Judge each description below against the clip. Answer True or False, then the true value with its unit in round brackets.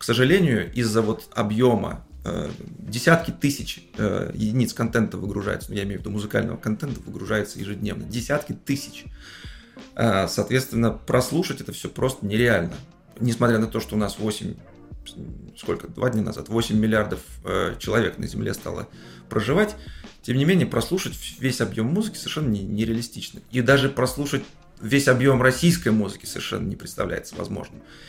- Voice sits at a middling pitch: False (115 Hz)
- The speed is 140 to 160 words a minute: True (150 wpm)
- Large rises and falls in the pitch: False (4.1 semitones)